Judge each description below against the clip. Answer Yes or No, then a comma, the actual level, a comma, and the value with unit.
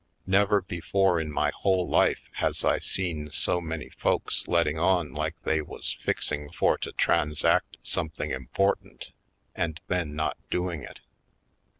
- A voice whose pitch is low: Yes, very low, 80 Hz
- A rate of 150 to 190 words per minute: No, average, 140 wpm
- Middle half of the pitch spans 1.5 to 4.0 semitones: Yes, average, 3.2 semitones